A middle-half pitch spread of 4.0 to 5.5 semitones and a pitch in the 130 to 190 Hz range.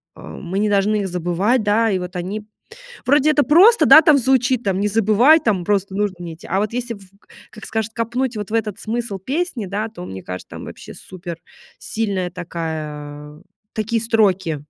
No: average, 4.3 semitones; high, 205 Hz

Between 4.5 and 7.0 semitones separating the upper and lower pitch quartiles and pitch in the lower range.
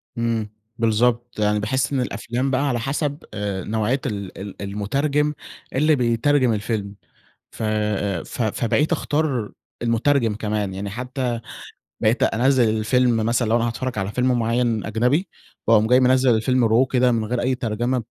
No: average, 3.1 semitones; low, 120 Hz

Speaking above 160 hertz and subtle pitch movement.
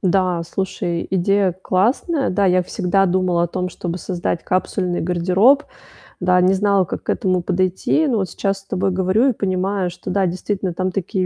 Yes: medium, 185 Hz; narrow, 1.5 semitones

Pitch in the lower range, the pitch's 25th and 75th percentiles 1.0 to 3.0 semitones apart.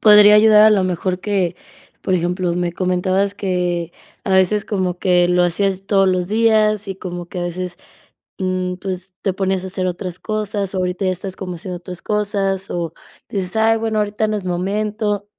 No: high, 190 Hz; narrow, 2.4 semitones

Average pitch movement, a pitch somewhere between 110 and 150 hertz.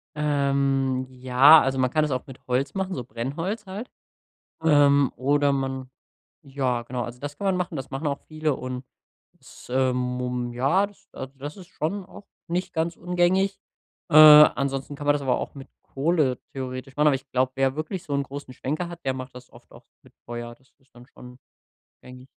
Yes: average, 3.2 semitones; medium, 140 Hz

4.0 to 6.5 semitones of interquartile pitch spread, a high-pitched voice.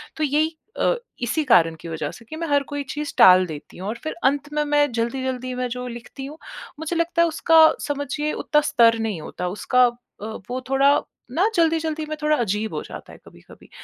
Yes: average, 4.8 semitones; very high, 275 Hz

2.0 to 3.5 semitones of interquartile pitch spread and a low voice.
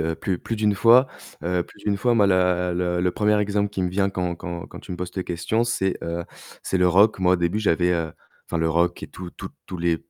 Yes: average, 2.7 semitones; very low, 90 Hz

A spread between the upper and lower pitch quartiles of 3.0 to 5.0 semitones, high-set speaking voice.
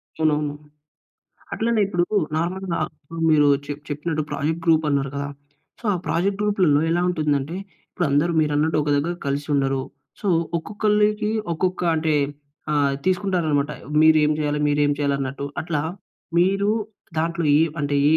No: average, 3.6 semitones; medium, 155 Hz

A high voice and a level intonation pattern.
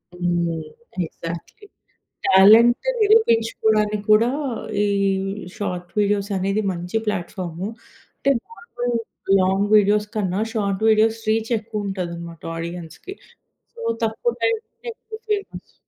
No: high, 210 Hz; average, 4.0 semitones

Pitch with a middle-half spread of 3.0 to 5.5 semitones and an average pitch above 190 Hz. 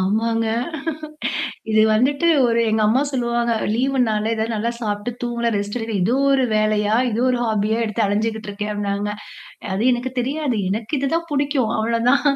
No: narrow, 2.5 semitones; high, 225 Hz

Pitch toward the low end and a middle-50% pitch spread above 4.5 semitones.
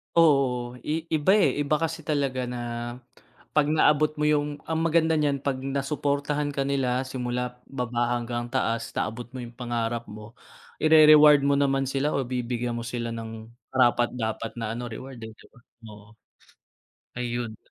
No: low, 130 Hz; average, 3.4 semitones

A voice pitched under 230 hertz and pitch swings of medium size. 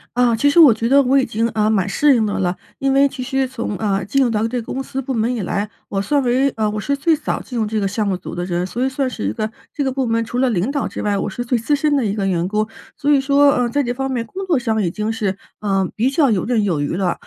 No: high, 235 Hz; average, 4.4 semitones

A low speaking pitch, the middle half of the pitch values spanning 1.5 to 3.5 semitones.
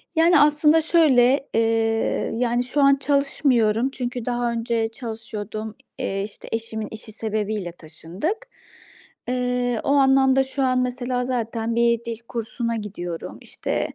No: high, 240 Hz; average, 3.1 semitones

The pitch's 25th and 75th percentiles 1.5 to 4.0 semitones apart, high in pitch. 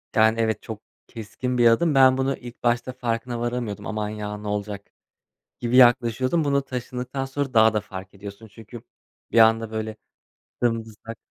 No: narrow, 2.6 semitones; low, 115 Hz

